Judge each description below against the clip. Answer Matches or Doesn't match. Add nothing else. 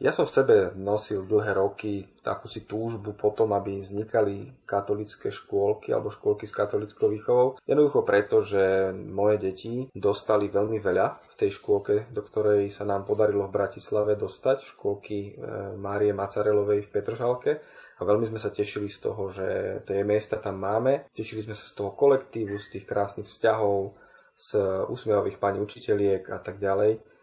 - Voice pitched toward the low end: Matches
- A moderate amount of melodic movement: Matches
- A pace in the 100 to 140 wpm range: Doesn't match